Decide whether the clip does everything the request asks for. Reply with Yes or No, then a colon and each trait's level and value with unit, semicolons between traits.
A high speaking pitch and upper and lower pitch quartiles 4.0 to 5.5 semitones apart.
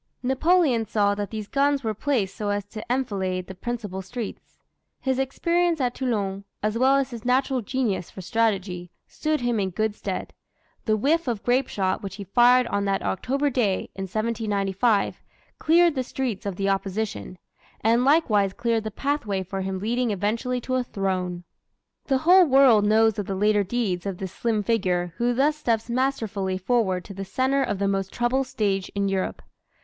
Yes: high, 220 Hz; average, 4.7 semitones